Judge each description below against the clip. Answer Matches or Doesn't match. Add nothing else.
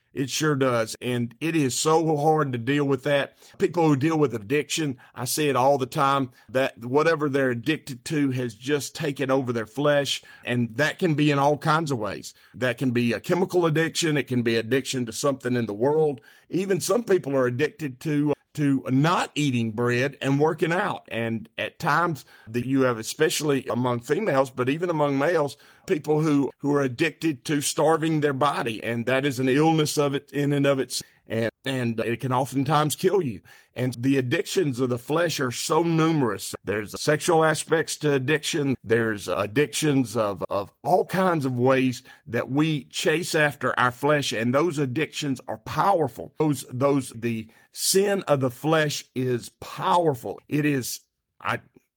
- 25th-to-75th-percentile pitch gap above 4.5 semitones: Doesn't match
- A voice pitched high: Doesn't match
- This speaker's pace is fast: Doesn't match